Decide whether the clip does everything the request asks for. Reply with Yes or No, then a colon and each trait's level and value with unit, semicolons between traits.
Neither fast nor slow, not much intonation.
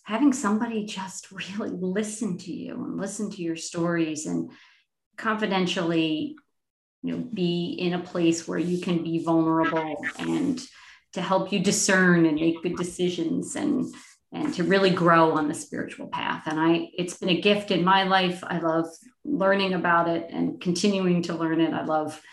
No: average, 170 wpm; average, 3.5 semitones